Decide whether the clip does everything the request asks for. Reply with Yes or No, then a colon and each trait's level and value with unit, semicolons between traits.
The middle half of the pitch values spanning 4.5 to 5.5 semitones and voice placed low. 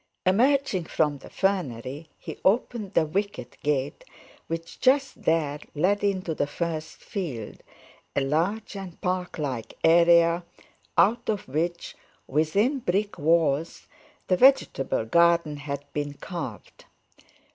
No: average, 4.9 semitones; medium, 170 Hz